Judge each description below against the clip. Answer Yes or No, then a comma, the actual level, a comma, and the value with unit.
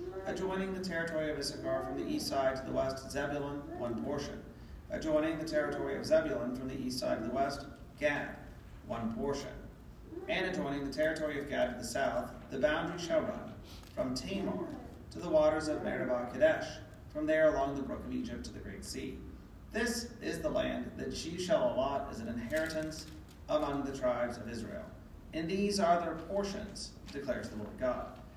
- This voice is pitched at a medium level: Yes, medium, 165 Hz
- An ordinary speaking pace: Yes, average, 185 wpm